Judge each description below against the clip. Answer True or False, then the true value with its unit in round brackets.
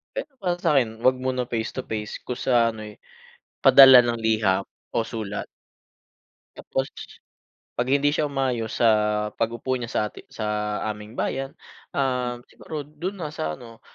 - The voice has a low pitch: True (125 Hz)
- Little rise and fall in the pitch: False (3.3 semitones)